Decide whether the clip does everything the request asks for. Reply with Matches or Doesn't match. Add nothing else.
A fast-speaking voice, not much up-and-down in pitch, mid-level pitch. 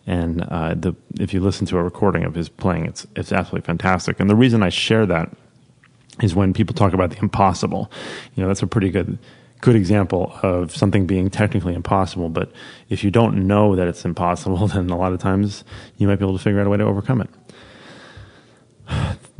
Doesn't match